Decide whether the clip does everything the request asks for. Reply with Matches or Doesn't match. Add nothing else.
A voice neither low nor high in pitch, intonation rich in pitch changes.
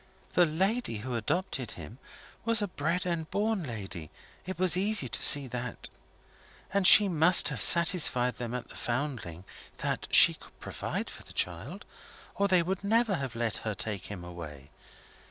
Matches